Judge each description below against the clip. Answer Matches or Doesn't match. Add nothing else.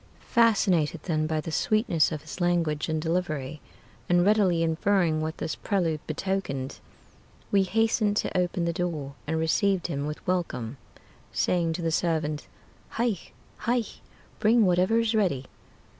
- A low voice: Doesn't match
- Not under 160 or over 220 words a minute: Doesn't match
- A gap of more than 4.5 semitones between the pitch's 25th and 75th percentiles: Doesn't match